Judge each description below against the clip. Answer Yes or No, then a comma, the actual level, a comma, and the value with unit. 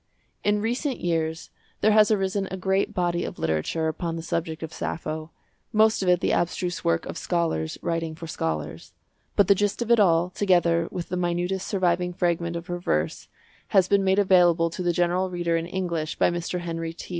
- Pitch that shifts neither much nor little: No, narrow, 2.3 semitones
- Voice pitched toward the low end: No, medium, 175 Hz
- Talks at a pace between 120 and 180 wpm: No, average, 195 wpm